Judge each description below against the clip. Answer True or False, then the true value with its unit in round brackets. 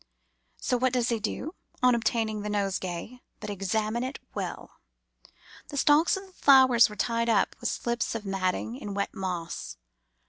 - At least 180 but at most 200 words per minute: False (165 wpm)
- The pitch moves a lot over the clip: False (3.8 semitones)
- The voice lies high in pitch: True (225 Hz)